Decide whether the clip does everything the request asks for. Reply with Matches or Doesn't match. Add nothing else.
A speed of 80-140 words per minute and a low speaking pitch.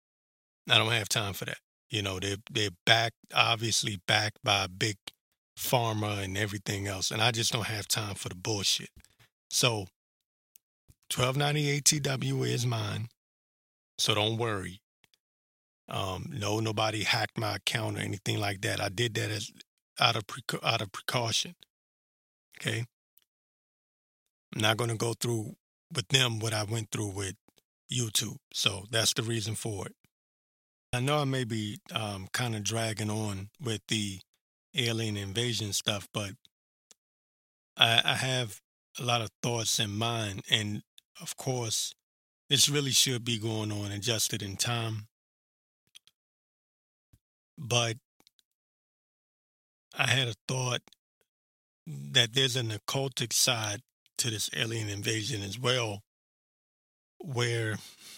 Matches